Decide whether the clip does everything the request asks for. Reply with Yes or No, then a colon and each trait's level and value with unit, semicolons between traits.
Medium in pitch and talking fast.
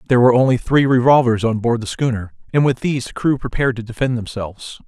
No: low, 120 Hz; fast, 220 wpm